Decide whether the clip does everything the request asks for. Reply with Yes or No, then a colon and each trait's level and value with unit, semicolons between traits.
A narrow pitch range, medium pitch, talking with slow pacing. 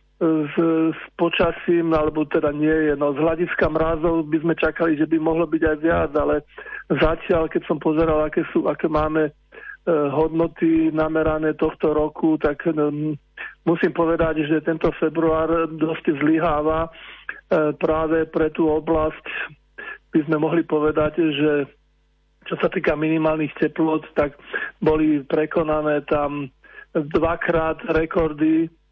No: narrow, 1.2 semitones; medium, 160 Hz; average, 135 wpm